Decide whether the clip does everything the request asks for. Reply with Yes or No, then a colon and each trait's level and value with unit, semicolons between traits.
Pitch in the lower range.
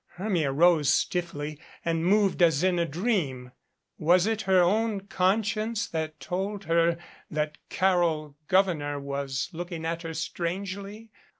No: medium, 175 Hz